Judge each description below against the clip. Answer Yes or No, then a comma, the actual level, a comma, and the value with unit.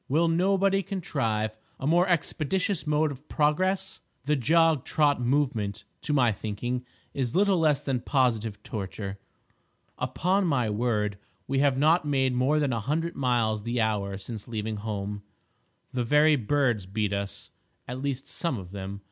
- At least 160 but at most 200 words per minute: No, average, 150 wpm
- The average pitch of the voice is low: Yes, low, 130 Hz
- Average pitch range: No, wide, 6.0 semitones